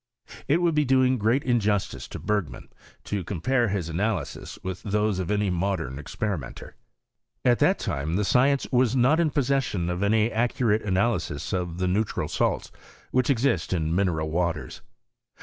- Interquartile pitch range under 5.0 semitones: No, wide, 5.6 semitones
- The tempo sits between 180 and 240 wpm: No, average, 160 wpm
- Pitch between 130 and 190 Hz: No, low, 105 Hz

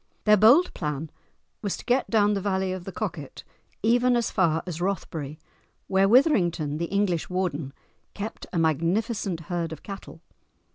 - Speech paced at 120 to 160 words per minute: Yes, average, 155 wpm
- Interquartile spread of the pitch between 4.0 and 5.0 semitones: Yes, average, 4.5 semitones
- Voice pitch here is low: No, medium, 185 Hz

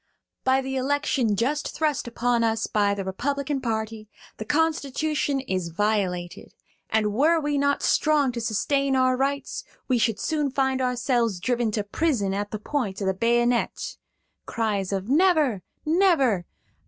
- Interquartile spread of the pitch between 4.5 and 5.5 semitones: Yes, average, 4.9 semitones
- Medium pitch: No, high, 245 Hz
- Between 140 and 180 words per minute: Yes, average, 150 wpm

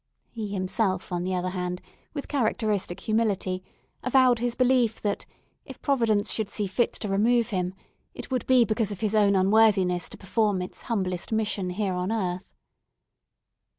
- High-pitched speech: Yes, high, 205 Hz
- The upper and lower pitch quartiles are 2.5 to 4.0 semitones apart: Yes, average, 3.5 semitones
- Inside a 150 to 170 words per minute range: Yes, average, 160 wpm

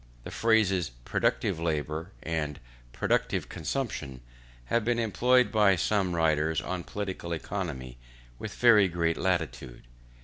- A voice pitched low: Yes, very low, 85 Hz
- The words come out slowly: Yes, slow, 115 wpm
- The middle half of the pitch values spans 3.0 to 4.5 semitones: No, average, 5.0 semitones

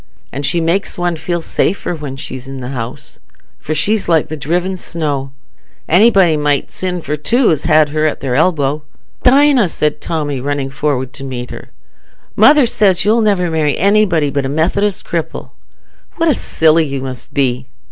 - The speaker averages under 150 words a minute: No, average, 175 wpm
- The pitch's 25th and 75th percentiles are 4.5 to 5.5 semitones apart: Yes, average, 5.0 semitones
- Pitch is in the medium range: Yes, medium, 155 Hz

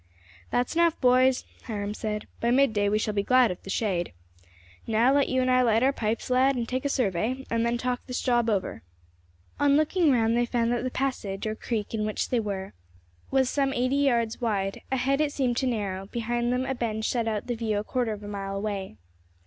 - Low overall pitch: No, high, 235 Hz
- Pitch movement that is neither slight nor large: Yes, average, 3.3 semitones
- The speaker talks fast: Yes, fast, 220 wpm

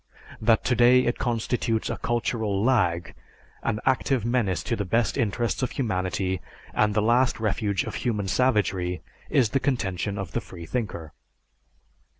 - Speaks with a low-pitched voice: Yes, low, 110 Hz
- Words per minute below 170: Yes, average, 145 wpm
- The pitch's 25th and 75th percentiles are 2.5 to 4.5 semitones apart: Yes, average, 4.0 semitones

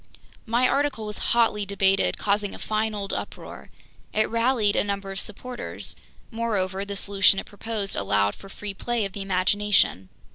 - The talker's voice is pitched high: Yes, high, 205 Hz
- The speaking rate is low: No, average, 160 wpm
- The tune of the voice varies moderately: No, narrow, 2.2 semitones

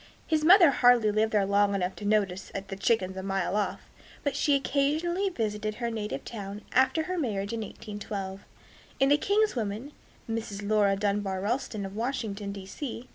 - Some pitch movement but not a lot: Yes, average, 4.8 semitones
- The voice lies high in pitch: Yes, high, 215 Hz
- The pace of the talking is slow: No, average, 170 wpm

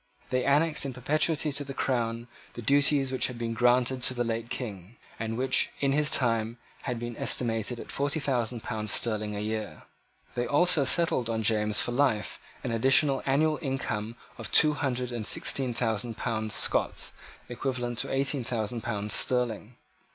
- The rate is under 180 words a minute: Yes, average, 170 wpm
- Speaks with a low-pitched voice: Yes, low, 120 Hz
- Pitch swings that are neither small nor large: Yes, average, 3.2 semitones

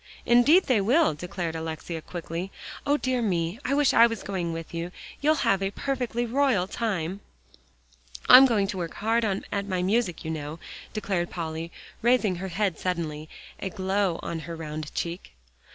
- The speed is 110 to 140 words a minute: No, average, 170 wpm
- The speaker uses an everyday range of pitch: No, wide, 5.7 semitones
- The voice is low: No, high, 190 Hz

